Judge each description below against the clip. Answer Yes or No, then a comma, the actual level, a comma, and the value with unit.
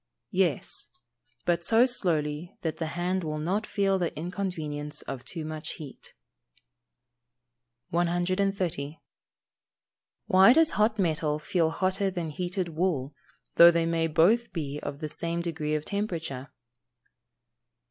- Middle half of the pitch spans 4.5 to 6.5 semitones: No, average, 3.6 semitones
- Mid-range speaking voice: Yes, medium, 170 Hz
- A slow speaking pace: Yes, slow, 125 wpm